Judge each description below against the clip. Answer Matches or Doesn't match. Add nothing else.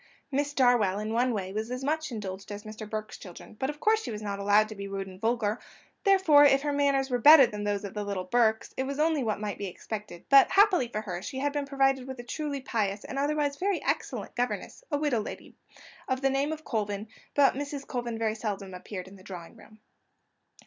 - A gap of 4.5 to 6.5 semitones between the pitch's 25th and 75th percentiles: Matches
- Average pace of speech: Doesn't match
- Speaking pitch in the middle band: Doesn't match